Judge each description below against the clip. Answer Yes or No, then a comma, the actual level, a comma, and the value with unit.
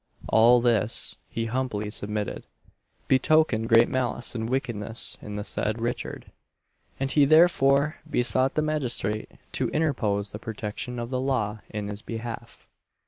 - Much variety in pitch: No, average, 3.6 semitones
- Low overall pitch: Yes, low, 120 Hz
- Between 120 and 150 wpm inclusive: Yes, average, 140 wpm